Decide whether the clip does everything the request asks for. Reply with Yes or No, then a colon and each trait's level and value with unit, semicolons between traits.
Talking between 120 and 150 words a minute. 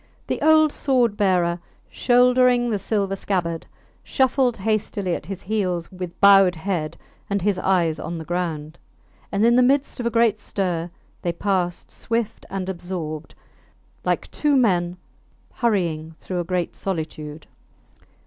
Yes: average, 140 wpm